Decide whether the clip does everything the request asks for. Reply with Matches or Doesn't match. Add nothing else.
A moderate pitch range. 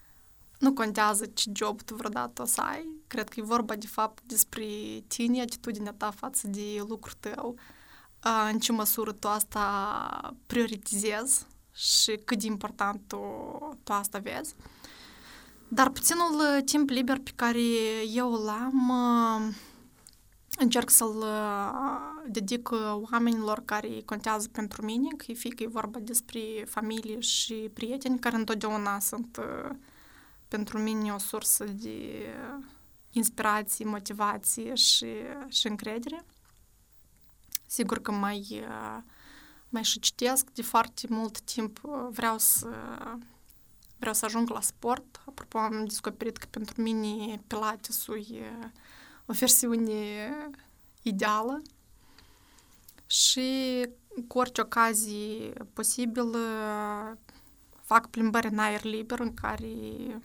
Doesn't match